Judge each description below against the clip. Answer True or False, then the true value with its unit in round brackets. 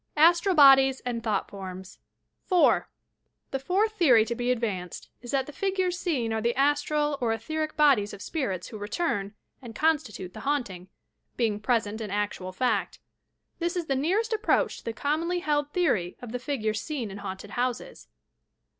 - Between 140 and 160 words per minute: False (175 wpm)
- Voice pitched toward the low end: False (255 Hz)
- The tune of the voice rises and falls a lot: True (6.5 semitones)